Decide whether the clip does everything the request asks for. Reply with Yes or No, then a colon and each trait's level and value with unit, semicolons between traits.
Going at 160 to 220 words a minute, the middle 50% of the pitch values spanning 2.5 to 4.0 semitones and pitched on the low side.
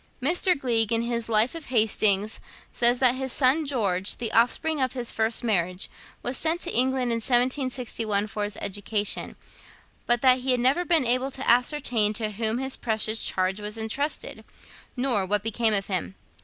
No: average, 175 wpm; average, 3.5 semitones; high, 235 Hz